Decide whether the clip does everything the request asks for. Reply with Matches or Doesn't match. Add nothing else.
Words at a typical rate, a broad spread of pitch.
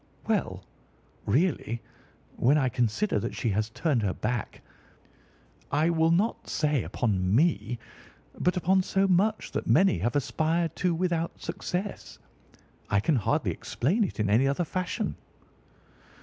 Doesn't match